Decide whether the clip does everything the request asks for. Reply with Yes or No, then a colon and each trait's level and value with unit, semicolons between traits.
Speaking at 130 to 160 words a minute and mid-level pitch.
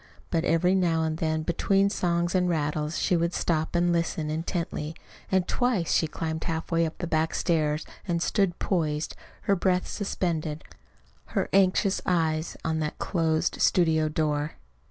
Yes: average, 155 wpm; medium, 165 Hz